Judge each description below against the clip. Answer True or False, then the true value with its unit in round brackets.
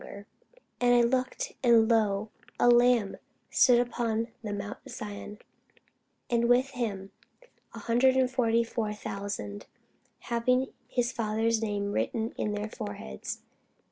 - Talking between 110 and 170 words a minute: True (140 wpm)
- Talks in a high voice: True (230 Hz)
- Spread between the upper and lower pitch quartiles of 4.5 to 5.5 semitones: False (2.8 semitones)